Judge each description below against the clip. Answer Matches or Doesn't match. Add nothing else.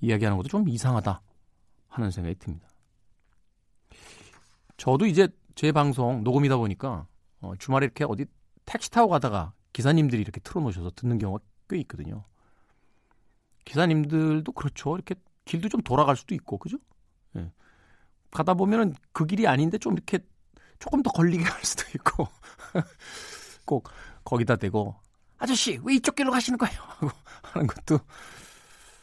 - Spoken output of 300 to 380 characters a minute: Matches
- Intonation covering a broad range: Matches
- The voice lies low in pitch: Matches